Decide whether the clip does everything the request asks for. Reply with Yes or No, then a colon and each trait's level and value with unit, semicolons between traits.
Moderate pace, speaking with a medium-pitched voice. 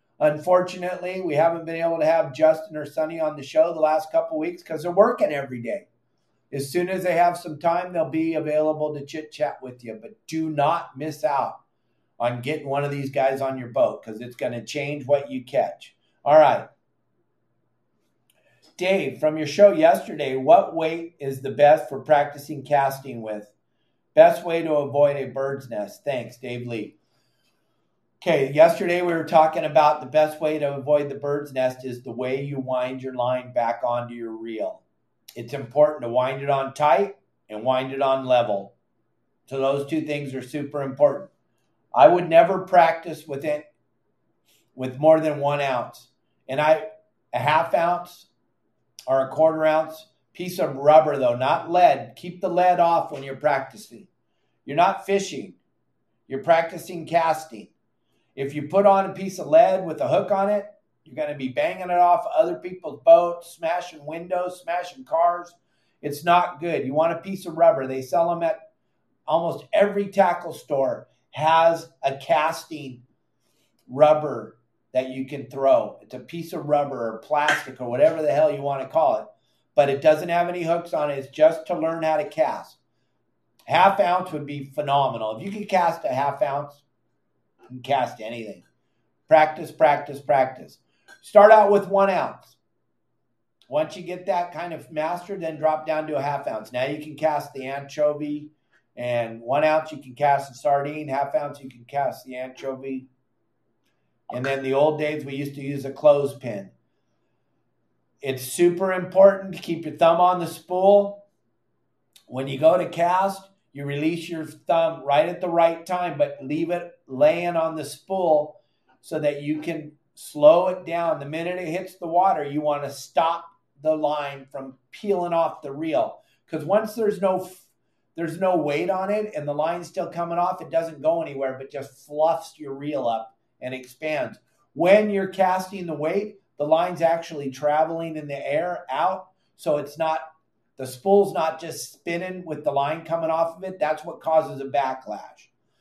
Yes: average, 180 wpm; medium, 155 Hz